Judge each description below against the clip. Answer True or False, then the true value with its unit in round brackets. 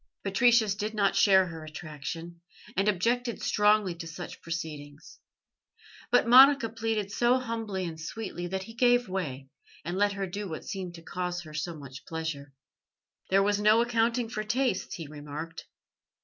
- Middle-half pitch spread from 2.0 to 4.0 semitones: False (5.3 semitones)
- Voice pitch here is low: False (190 Hz)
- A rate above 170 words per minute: False (160 wpm)